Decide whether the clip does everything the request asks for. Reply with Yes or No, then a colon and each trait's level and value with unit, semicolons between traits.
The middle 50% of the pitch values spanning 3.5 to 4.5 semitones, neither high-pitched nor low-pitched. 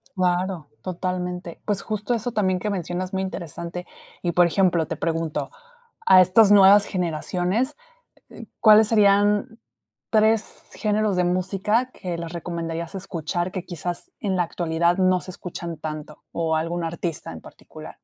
No: average, 3.0 semitones; medium, 180 Hz